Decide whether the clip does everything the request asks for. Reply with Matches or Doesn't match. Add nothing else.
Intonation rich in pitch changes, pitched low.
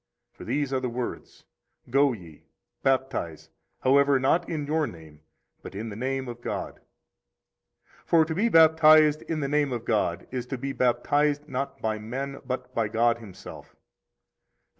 Doesn't match